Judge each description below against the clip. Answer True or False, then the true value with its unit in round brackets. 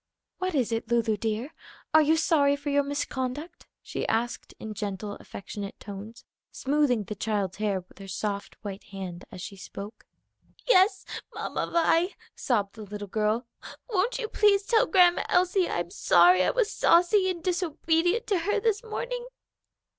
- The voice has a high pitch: True (265 Hz)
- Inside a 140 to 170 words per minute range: True (160 wpm)